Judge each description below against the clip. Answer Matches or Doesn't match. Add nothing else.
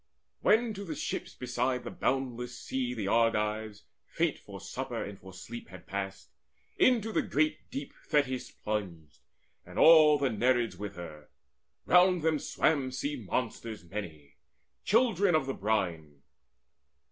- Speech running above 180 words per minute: Doesn't match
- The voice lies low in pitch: Matches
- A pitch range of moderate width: Doesn't match